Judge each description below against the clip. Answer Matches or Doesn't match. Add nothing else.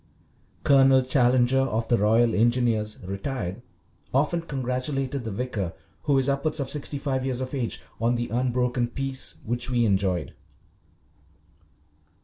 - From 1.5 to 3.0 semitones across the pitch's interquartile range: Matches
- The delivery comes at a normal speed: Doesn't match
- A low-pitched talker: Matches